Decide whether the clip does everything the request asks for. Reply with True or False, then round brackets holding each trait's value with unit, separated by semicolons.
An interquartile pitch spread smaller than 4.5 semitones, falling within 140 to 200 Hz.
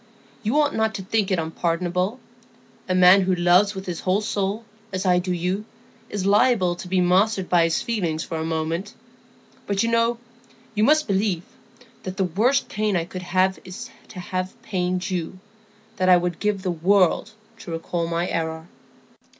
True (3.1 semitones; 185 Hz)